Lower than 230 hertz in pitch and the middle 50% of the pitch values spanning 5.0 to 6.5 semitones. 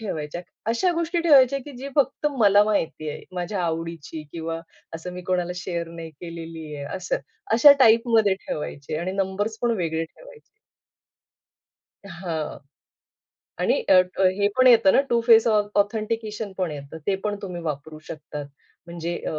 Yes: medium, 185 Hz; wide, 5.4 semitones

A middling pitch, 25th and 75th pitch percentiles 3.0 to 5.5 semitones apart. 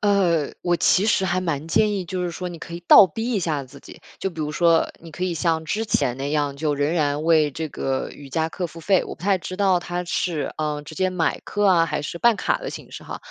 Yes: medium, 170 Hz; average, 3.5 semitones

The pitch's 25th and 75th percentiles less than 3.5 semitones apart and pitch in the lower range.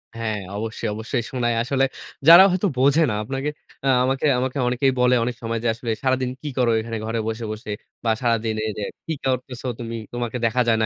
Yes: narrow, 2.5 semitones; low, 120 Hz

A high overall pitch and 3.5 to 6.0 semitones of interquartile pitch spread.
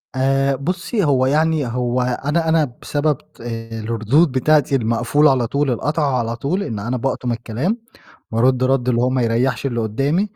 No: low, 130 Hz; average, 3.8 semitones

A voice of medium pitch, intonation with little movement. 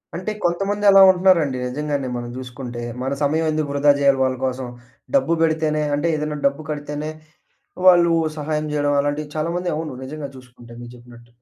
No: medium, 150 Hz; average, 3.4 semitones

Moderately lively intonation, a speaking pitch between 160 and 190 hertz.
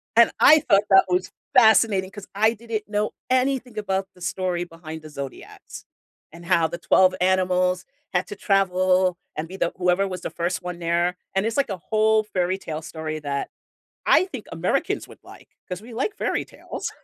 Yes: average, 3.4 semitones; medium, 185 Hz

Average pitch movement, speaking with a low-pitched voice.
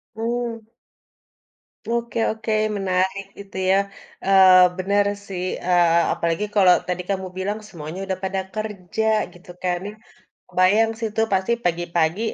No: average, 3.1 semitones; high, 190 Hz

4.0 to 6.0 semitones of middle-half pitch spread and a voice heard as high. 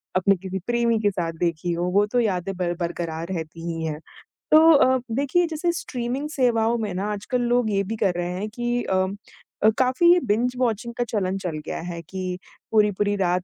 Yes: average, 5.2 semitones; high, 205 Hz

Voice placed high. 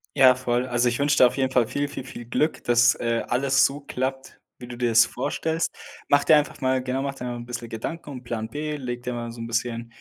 No: low, 125 Hz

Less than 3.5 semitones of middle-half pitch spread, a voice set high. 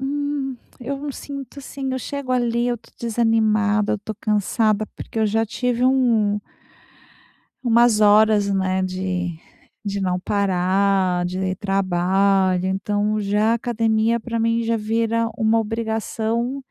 Yes: average, 3.0 semitones; high, 220 Hz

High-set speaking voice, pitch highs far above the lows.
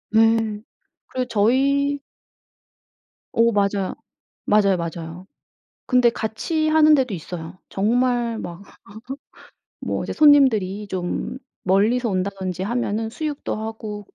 No: high, 220 Hz; average, 4.4 semitones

